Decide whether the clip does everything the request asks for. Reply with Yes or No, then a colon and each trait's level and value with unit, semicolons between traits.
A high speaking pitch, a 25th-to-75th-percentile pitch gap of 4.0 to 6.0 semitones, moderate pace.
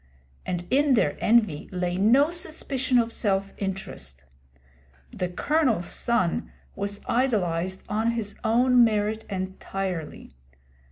No: high, 210 Hz; average, 4.4 semitones; slow, 110 wpm